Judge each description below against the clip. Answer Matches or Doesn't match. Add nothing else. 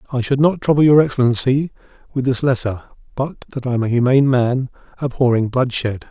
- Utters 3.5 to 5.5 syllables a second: Doesn't match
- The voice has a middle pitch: Doesn't match